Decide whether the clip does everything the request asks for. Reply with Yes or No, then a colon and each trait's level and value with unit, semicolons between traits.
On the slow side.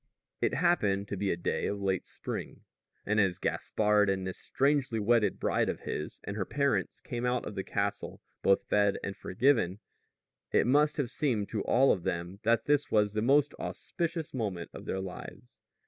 No: average, 185 wpm